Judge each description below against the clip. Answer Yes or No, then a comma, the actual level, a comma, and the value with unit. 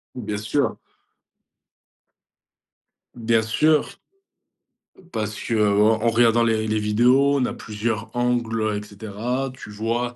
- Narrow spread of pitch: Yes, narrow, 2.2 semitones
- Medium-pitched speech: No, low, 115 Hz